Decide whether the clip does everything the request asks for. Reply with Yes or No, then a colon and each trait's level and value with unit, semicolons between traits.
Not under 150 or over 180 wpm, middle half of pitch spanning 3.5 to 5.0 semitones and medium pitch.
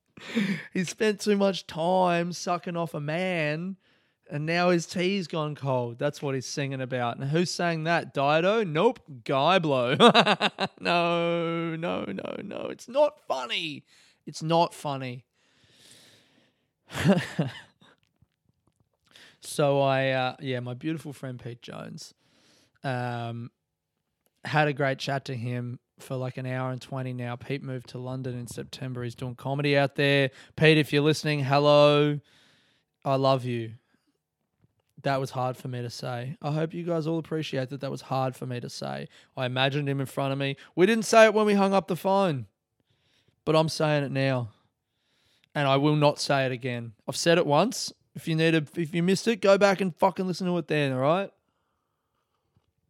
Yes: average, 170 wpm; average, 4.6 semitones; medium, 145 Hz